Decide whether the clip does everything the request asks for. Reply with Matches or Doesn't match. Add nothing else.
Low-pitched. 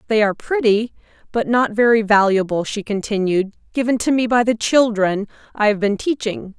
Doesn't match